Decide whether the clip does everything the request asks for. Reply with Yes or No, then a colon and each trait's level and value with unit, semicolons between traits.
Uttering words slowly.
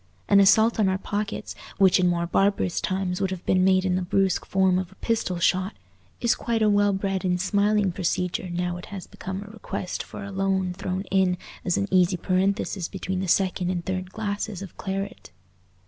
No: average, 200 wpm